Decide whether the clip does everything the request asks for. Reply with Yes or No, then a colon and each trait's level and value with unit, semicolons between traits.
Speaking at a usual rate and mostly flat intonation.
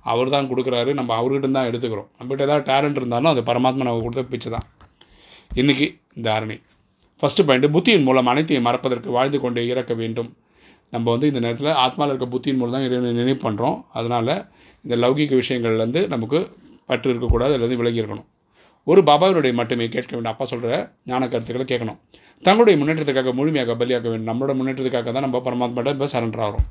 No: fast, 160 wpm; narrow, 2.3 semitones